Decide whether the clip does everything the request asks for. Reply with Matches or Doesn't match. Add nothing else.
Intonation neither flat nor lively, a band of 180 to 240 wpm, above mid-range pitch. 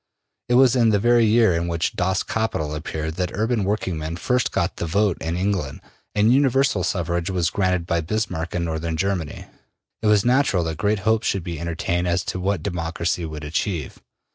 Doesn't match